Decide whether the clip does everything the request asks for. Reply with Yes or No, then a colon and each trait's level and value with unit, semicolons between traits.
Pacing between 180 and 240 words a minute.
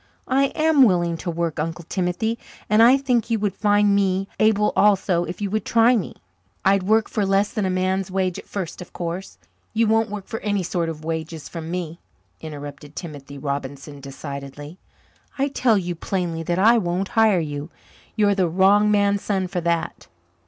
Yes: average, 185 wpm